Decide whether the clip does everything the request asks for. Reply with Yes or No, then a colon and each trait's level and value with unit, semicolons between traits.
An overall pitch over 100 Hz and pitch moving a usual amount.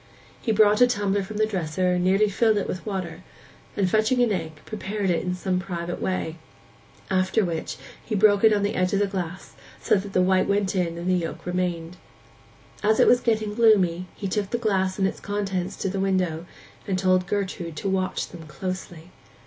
No: high, 190 Hz; narrow, 2.3 semitones